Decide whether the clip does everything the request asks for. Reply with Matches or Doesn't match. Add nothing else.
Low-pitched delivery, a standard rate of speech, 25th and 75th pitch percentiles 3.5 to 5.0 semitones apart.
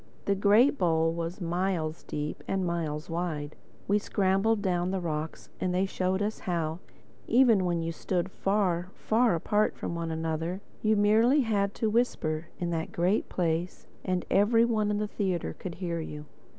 Doesn't match